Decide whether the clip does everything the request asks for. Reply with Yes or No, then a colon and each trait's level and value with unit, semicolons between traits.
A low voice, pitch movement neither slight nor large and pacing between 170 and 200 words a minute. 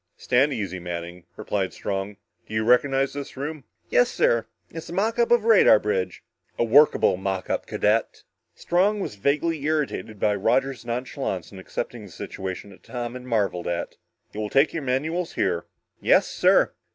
No: low, 120 Hz; wide, 6.7 semitones; average, 175 wpm